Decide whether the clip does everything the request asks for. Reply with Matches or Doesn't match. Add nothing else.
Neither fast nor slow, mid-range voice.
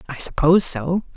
Matches